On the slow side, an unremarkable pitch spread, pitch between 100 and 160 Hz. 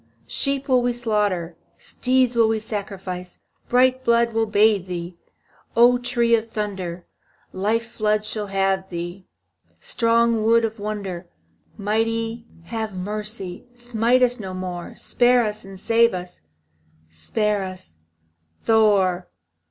No: slow, 125 wpm; average, 3.6 semitones; high, 215 Hz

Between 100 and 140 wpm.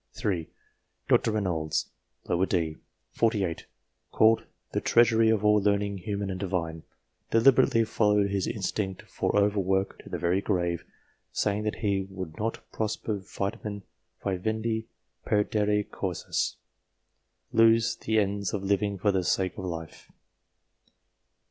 Yes: slow, 135 wpm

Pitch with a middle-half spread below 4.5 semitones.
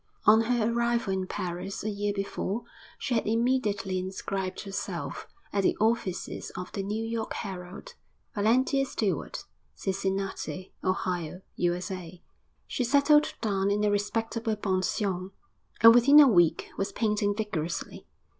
Yes: average, 3.3 semitones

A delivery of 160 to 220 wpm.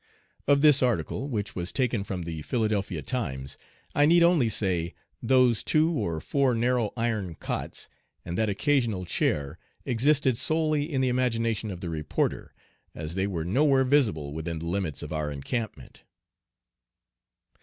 No: average, 150 wpm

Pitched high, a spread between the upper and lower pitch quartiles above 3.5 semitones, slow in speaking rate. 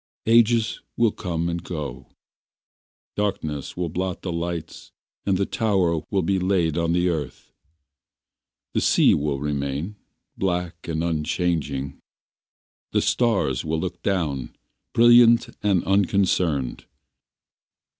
No: very low, 85 Hz; average, 4.1 semitones; slow, 115 wpm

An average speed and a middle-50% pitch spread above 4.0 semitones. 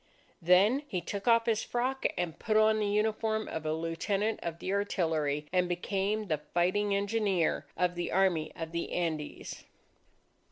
Yes: average, 155 wpm; average, 4.4 semitones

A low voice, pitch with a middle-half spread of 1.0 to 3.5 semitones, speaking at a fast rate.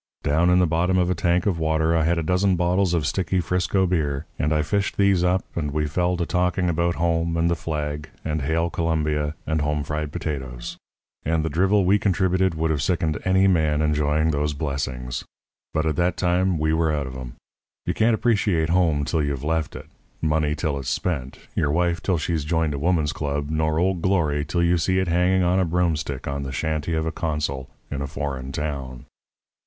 Yes: very low, 80 Hz; average, 3.1 semitones; fast, 210 wpm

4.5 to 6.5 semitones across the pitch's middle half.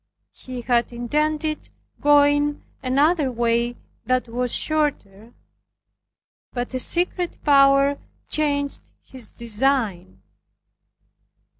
No: average, 3.5 semitones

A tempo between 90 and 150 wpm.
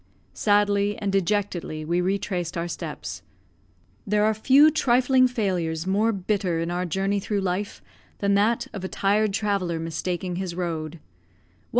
Yes: average, 140 wpm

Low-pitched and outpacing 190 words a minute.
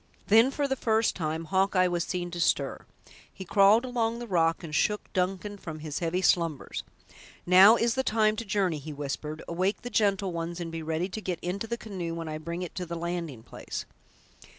No: medium, 180 Hz; fast, 205 wpm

